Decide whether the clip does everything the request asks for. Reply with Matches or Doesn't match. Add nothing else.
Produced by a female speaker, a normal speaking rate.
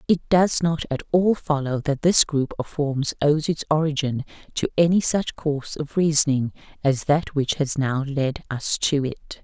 Matches